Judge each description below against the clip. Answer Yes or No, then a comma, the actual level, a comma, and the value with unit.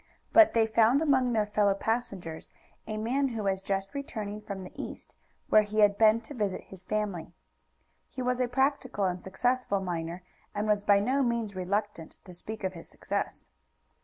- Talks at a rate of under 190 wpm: Yes, average, 180 wpm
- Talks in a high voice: Yes, high, 210 Hz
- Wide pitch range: No, average, 3.8 semitones